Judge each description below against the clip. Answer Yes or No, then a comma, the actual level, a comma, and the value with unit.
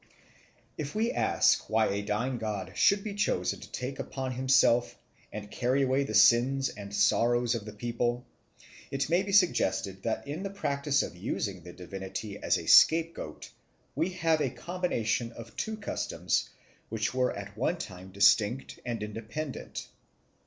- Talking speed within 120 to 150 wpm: No, average, 160 wpm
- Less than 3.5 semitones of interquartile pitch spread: No, average, 5.3 semitones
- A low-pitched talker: Yes, low, 120 Hz